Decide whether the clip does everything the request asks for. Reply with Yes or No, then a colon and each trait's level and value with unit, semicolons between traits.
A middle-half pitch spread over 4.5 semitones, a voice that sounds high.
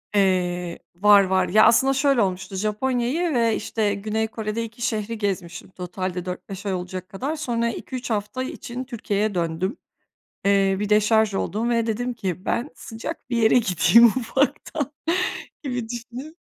No: average, 3.8 semitones; high, 215 Hz